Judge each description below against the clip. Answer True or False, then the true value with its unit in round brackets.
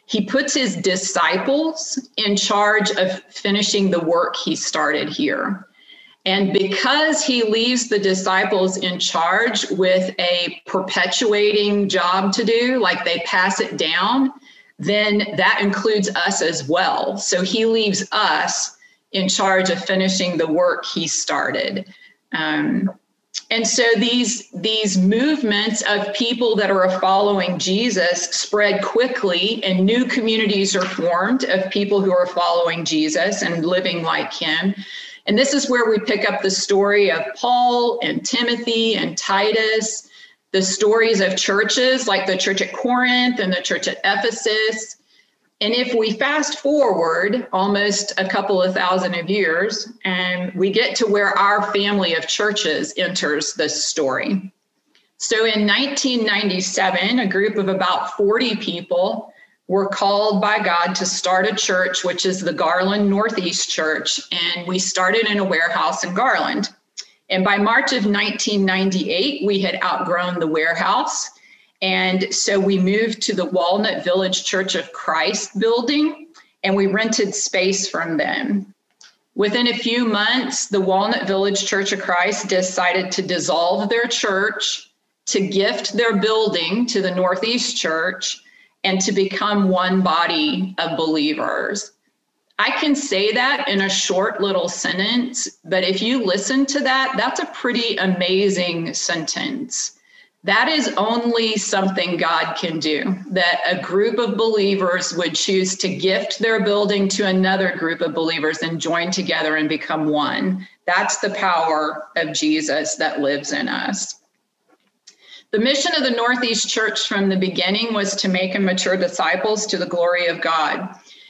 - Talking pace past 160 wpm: False (150 wpm)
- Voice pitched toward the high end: True (200 Hz)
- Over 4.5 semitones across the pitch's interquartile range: False (3.4 semitones)